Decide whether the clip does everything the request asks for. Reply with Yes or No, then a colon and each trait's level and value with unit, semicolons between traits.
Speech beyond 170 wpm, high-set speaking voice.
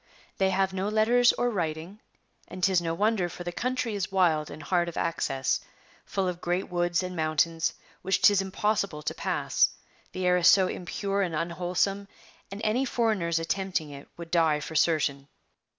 No: average, 180 wpm; medium, 180 Hz